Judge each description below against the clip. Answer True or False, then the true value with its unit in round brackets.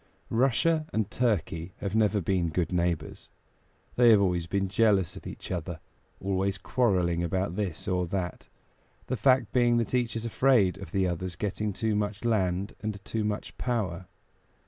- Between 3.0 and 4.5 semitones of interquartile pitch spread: True (3.7 semitones)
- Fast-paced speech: False (165 wpm)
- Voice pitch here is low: True (100 Hz)